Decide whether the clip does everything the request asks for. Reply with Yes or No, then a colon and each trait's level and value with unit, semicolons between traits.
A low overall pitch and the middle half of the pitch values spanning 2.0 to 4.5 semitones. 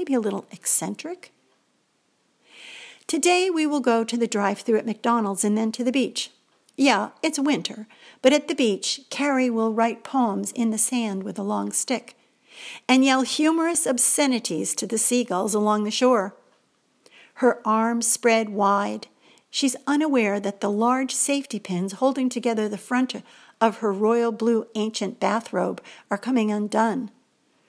No: high, 235 Hz; average, 3.6 semitones